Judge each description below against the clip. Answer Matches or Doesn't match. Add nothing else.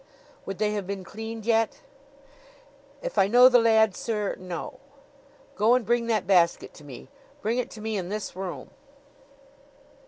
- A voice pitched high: Matches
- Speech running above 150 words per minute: Matches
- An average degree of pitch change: Matches